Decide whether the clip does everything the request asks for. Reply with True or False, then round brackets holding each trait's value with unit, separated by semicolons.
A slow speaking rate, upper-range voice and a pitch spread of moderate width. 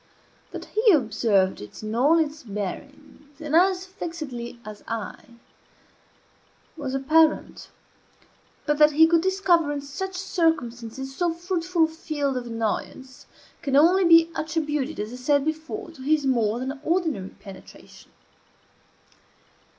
True (130 wpm; 295 Hz; 4.8 semitones)